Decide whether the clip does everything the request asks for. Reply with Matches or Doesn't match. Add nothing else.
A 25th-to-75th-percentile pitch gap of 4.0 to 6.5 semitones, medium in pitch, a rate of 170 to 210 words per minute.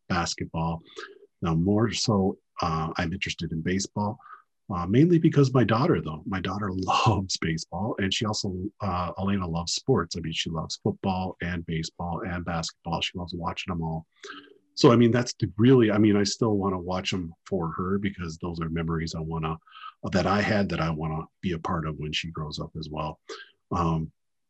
Doesn't match